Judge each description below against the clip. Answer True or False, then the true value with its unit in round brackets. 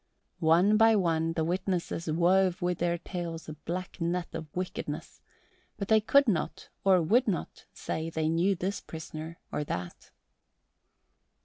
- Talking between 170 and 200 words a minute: False (145 wpm)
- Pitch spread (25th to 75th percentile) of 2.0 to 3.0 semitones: True (2.7 semitones)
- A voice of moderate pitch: True (175 Hz)